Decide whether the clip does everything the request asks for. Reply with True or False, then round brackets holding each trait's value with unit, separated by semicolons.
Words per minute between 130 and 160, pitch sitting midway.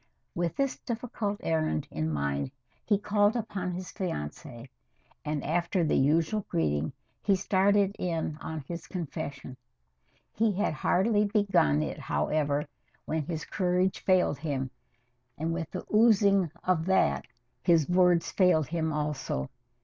True (135 wpm; 170 Hz)